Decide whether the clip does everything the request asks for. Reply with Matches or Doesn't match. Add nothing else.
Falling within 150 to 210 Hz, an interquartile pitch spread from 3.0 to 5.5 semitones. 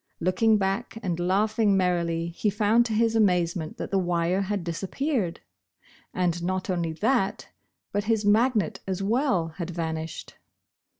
Matches